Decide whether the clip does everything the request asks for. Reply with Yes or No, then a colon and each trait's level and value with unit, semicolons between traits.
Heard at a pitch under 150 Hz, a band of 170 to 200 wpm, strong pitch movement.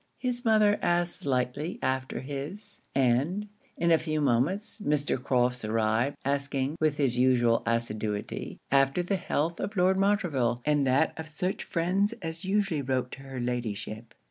No: medium, 140 Hz; average, 150 wpm; wide, 6.1 semitones